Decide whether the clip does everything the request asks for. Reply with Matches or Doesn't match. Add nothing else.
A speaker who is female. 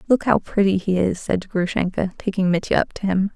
Matches